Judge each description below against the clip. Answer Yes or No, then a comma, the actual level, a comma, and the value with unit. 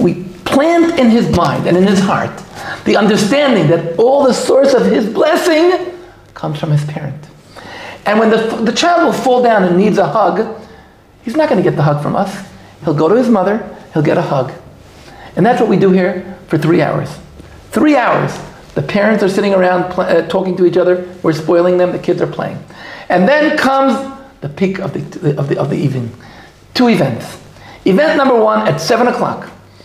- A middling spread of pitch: No, wide, 6.0 semitones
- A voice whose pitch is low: No, high, 190 Hz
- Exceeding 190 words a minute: Yes, average, 200 wpm